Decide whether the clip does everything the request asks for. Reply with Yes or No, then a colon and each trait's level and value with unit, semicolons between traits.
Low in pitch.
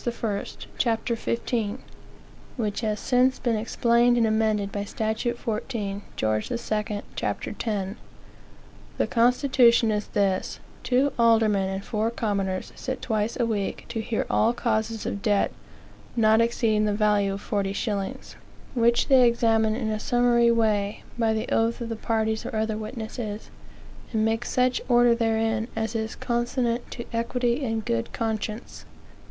No: high, 225 Hz